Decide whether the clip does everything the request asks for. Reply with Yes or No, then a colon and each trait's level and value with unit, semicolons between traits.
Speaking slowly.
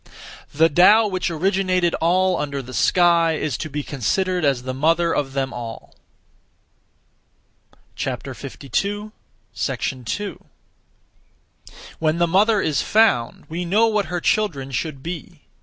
Yes: slow, 120 wpm